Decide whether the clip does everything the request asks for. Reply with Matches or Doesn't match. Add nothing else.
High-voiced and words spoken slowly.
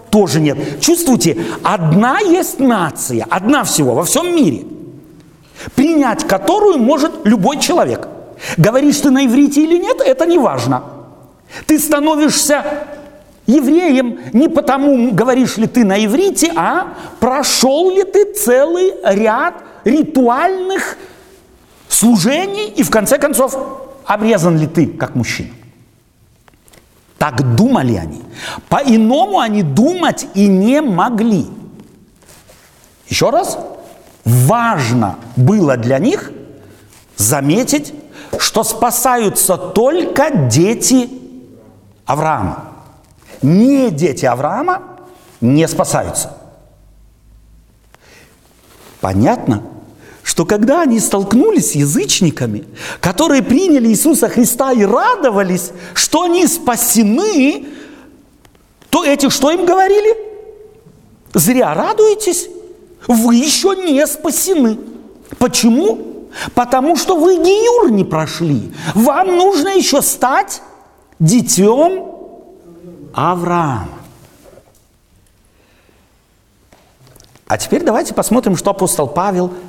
Matches